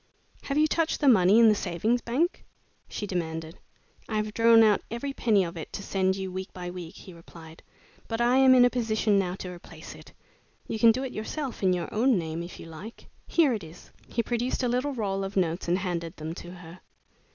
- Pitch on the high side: Yes, high, 200 Hz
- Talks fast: Yes, fast, 220 wpm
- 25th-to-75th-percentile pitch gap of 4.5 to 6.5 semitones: Yes, average, 5.2 semitones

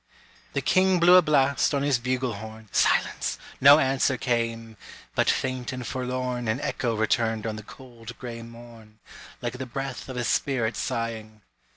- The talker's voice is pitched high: No, low, 120 Hz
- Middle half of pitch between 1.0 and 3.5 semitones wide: Yes, narrow, 2.6 semitones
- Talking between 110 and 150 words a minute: No, average, 165 wpm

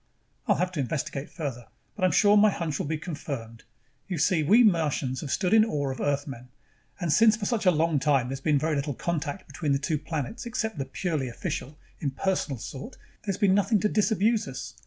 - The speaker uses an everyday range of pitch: No, wide, 6.0 semitones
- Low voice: No, medium, 155 Hz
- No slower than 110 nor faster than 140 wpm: No, average, 200 wpm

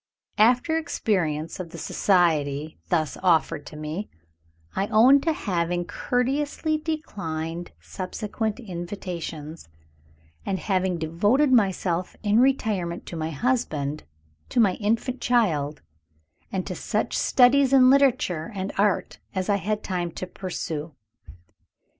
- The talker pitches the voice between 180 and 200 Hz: Yes, high, 190 Hz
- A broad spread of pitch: Yes, wide, 6.4 semitones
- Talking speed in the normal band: No, slow, 120 wpm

